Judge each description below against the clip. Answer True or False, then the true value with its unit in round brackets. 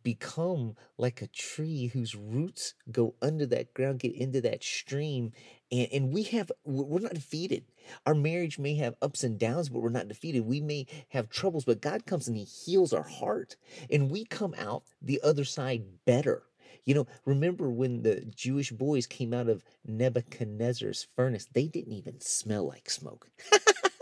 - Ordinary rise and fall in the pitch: True (3.8 semitones)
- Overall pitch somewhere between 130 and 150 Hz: True (135 Hz)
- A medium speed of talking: True (175 wpm)